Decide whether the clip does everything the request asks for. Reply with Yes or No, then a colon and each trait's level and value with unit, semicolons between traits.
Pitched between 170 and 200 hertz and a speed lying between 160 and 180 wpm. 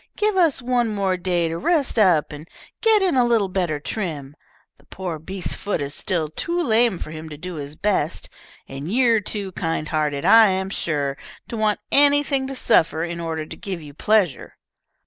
No: medium, 185 Hz; average, 190 wpm